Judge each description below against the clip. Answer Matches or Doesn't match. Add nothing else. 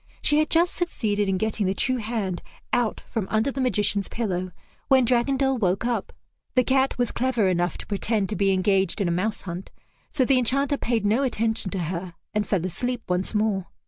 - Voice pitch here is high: Matches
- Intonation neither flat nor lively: Matches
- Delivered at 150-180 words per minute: Doesn't match